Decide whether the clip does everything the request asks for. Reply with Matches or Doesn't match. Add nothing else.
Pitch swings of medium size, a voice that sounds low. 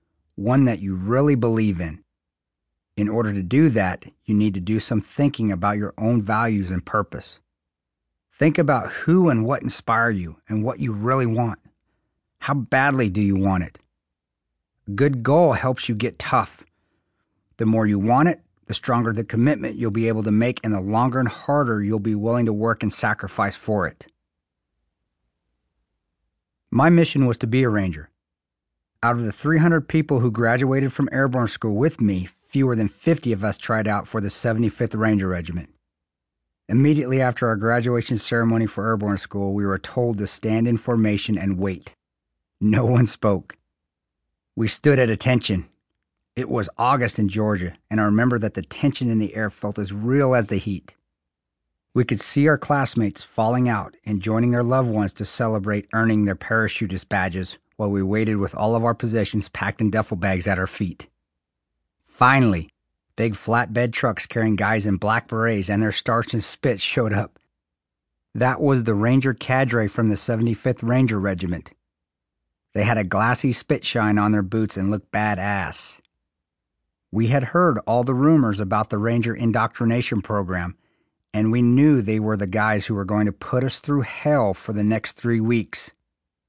Matches